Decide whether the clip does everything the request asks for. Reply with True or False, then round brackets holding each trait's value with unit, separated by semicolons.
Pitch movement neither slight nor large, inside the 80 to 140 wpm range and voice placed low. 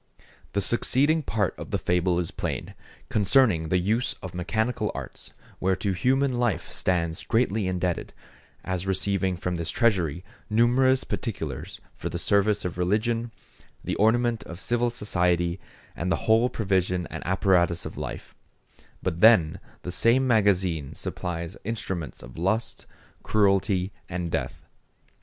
True (4.3 semitones; 135 wpm; 95 Hz)